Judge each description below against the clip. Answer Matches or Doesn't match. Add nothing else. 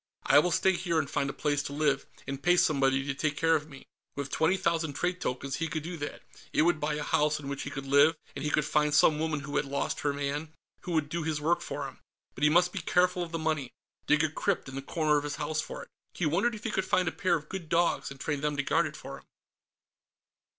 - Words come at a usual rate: Doesn't match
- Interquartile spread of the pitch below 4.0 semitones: Matches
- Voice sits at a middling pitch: Matches